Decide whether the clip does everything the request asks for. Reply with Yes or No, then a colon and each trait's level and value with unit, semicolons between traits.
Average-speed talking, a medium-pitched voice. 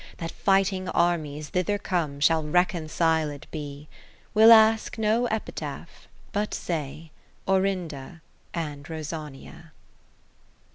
No: slow, 95 wpm; medium, 165 Hz